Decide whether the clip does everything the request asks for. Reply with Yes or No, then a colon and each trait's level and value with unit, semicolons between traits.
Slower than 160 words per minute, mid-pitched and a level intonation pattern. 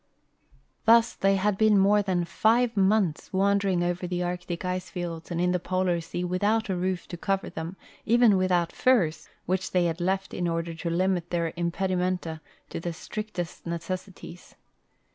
No: average, 170 wpm; medium, 180 Hz; narrow, 2.1 semitones